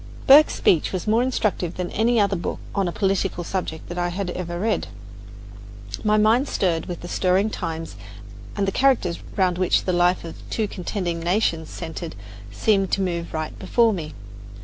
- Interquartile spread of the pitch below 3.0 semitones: No, average, 3.4 semitones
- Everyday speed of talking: Yes, average, 175 wpm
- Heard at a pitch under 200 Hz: Yes, medium, 185 Hz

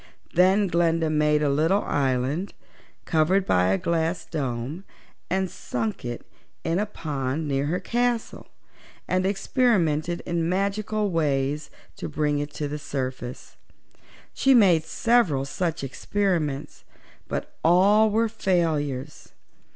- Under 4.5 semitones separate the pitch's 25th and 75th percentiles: No, average, 4.9 semitones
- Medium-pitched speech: Yes, medium, 165 Hz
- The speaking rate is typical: No, slow, 120 wpm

